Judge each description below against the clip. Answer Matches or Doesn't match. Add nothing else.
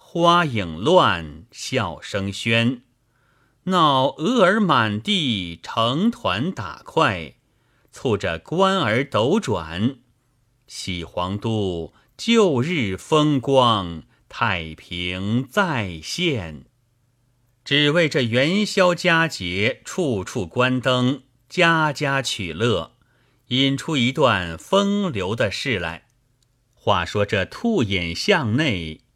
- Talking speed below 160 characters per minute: Matches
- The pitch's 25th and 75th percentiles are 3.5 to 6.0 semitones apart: Doesn't match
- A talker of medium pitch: Doesn't match